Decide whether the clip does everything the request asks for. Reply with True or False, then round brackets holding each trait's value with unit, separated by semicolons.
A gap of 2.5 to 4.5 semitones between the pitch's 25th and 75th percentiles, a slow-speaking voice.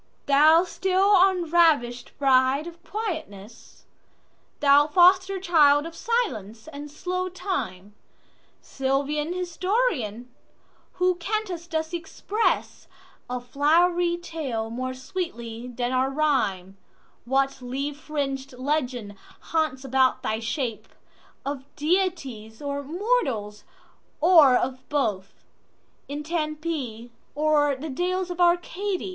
False (5.5 semitones; 90 wpm)